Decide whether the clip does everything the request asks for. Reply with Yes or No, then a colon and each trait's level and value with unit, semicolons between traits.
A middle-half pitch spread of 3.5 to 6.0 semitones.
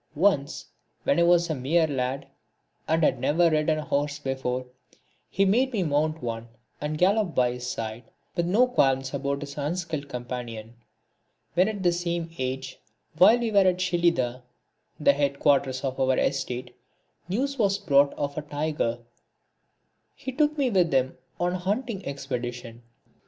Yes: average, 5.3 semitones